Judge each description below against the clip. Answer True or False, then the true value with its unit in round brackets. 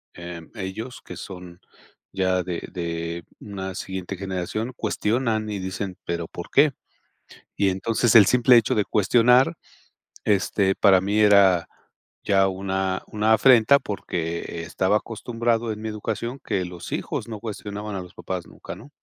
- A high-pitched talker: False (100 Hz)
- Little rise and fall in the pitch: False (3.1 semitones)